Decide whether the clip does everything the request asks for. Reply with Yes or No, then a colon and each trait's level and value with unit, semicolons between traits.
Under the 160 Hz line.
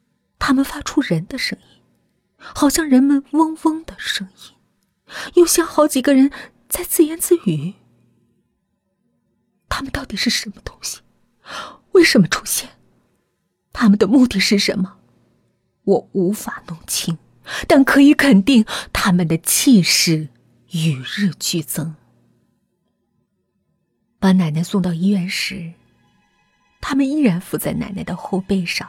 No: high, 205 Hz